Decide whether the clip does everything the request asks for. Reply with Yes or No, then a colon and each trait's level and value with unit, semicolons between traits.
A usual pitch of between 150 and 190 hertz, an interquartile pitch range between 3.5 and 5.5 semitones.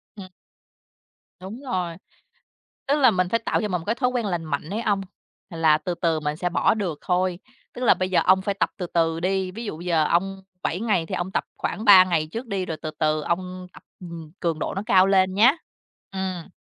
No: medium, 185 Hz; average, 2.9 semitones